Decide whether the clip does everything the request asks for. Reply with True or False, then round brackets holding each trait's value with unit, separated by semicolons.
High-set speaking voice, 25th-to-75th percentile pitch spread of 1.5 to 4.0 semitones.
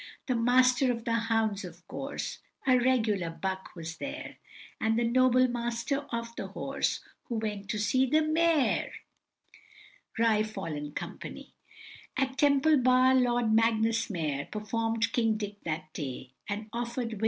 True (230 Hz; 3.3 semitones)